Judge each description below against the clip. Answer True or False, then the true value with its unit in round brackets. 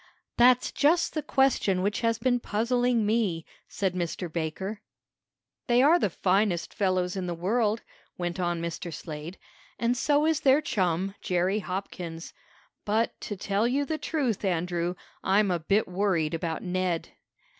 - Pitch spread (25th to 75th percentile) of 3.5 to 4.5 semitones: False (5.1 semitones)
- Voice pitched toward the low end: False (195 Hz)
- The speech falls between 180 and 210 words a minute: False (150 wpm)